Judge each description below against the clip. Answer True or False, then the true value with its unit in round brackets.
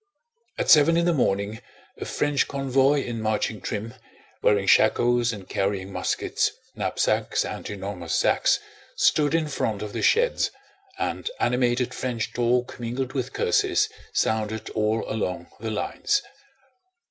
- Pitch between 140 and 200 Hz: False (120 Hz)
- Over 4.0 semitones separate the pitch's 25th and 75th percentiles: True (4.4 semitones)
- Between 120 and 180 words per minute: True (135 wpm)